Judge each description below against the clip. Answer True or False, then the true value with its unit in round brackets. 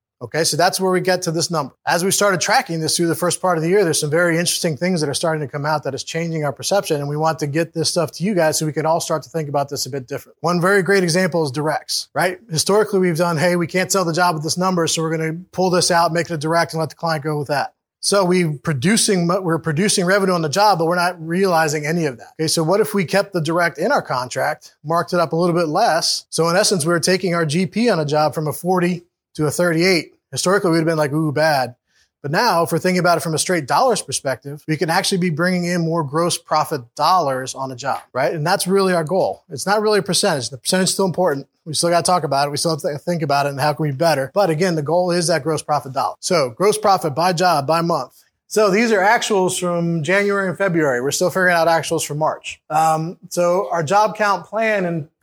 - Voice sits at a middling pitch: True (170 Hz)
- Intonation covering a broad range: False (2.8 semitones)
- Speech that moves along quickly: True (275 wpm)